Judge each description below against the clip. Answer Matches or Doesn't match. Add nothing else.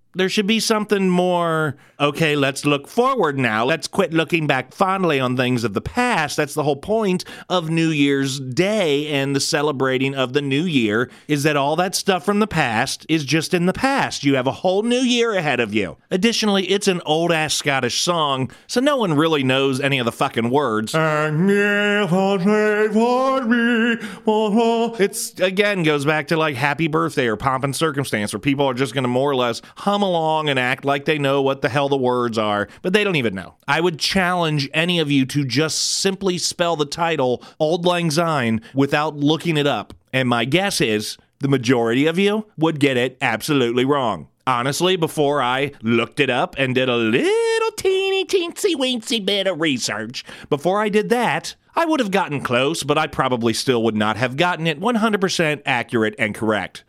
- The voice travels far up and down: Matches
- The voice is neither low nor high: Matches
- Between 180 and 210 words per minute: Matches